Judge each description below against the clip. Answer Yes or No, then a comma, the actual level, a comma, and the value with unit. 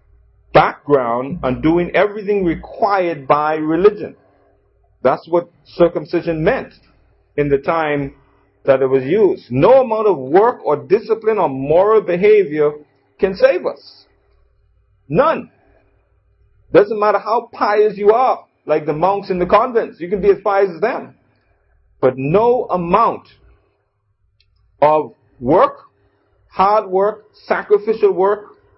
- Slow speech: Yes, slow, 125 wpm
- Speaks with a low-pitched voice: No, medium, 165 Hz